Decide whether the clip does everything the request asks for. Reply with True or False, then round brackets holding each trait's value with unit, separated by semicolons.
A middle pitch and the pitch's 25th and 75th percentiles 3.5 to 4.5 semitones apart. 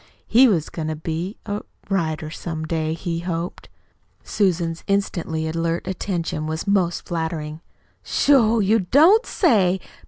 True (170 Hz; 3.9 semitones)